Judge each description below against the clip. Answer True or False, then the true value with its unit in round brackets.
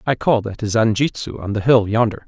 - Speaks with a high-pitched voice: False (115 Hz)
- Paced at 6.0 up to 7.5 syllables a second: True (6.2 syllables/s)